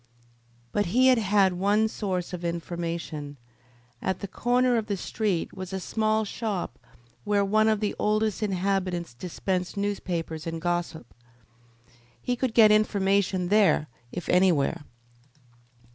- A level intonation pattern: No, average, 3.5 semitones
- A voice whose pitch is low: No, high, 195 Hz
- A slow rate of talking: Yes, slow, 130 wpm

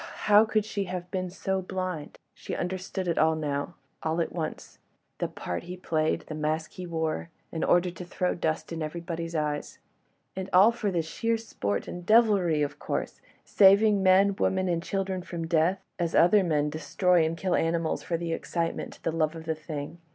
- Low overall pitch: No, medium, 170 Hz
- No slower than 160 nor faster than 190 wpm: Yes, average, 175 wpm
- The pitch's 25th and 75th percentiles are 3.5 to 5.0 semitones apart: No, average, 2.9 semitones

